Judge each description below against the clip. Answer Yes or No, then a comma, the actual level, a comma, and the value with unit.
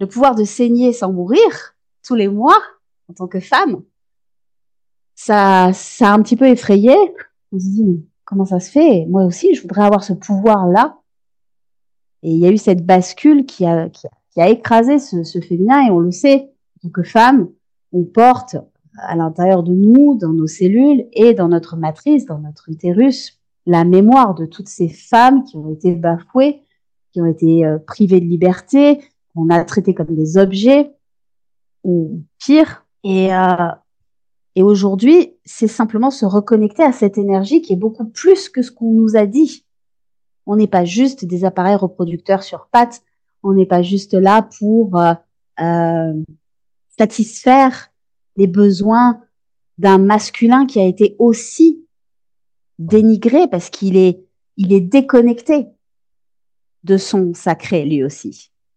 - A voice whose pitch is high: Yes, high, 200 Hz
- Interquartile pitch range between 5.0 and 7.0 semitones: Yes, wide, 5.4 semitones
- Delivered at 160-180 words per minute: Yes, average, 165 wpm